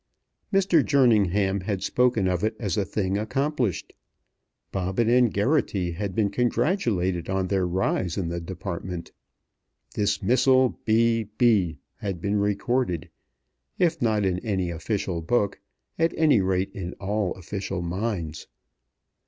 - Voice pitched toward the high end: No, low, 100 Hz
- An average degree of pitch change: Yes, average, 4.2 semitones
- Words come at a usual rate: No, slow, 130 wpm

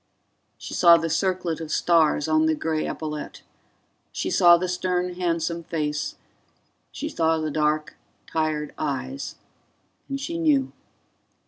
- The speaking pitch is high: No, medium, 165 Hz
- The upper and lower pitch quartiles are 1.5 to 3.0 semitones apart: Yes, narrow, 2.6 semitones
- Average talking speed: No, slow, 130 wpm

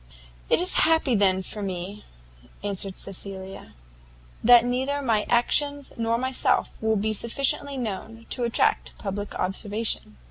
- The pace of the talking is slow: Yes, slow, 130 wpm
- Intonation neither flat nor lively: Yes, average, 4.1 semitones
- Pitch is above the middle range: Yes, high, 220 Hz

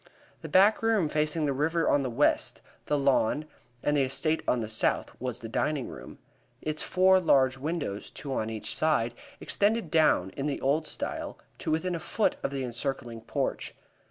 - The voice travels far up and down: No, average, 4.0 semitones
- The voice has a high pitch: No, medium, 145 Hz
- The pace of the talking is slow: No, average, 185 wpm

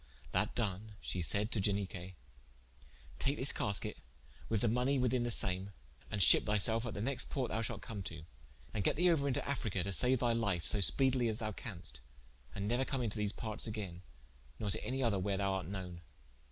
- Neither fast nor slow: No, fast, 210 wpm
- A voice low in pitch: Yes, low, 105 Hz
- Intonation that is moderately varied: Yes, average, 3.8 semitones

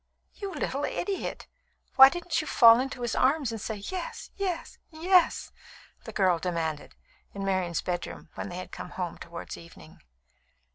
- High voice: Yes, high, 230 Hz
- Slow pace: No, average, 155 wpm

